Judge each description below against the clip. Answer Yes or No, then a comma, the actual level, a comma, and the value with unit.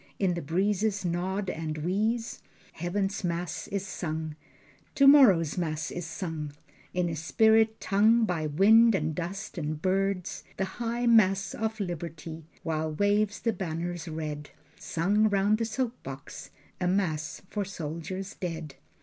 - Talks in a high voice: No, medium, 180 Hz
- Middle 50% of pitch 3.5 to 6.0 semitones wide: Yes, average, 4.3 semitones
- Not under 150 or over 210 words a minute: No, average, 140 wpm